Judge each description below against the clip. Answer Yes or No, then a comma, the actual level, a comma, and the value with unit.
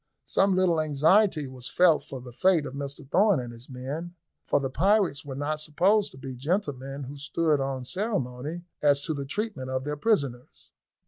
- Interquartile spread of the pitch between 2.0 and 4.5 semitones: No, average, 4.9 semitones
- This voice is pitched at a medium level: Yes, medium, 145 Hz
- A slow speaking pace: No, average, 185 wpm